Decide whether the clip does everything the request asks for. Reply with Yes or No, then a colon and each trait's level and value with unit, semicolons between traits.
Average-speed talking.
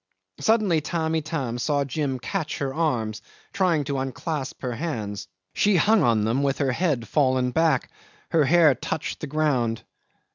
Yes: average, 155 wpm